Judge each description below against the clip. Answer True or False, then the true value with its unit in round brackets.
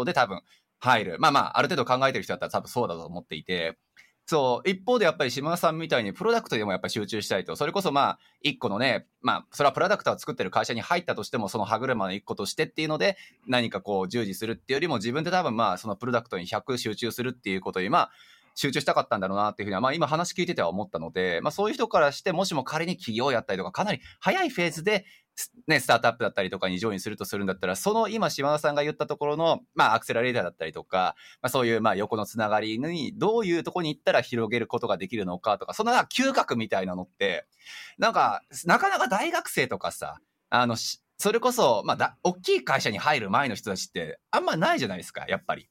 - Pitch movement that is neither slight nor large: False (8.2 semitones)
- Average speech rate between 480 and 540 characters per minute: True (510 characters per minute)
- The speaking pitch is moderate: False (130 Hz)